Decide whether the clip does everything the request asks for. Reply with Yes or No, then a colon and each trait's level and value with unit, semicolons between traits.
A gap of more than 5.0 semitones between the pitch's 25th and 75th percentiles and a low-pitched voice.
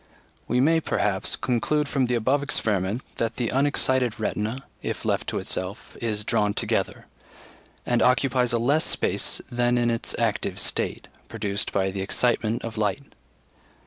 No: average, 3.4 semitones; low, 120 Hz